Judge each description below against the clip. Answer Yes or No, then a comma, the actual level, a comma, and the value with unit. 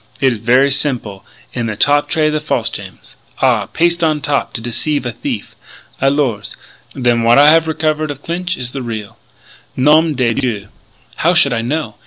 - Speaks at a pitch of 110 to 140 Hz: Yes, low, 135 Hz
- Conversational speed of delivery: Yes, average, 185 wpm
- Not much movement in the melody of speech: No, average, 4.7 semitones